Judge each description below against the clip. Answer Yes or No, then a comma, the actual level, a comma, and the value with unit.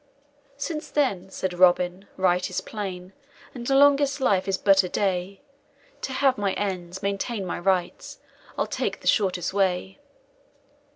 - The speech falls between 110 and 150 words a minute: Yes, average, 140 wpm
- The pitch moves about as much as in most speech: Yes, average, 4.6 semitones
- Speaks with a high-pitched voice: Yes, high, 195 Hz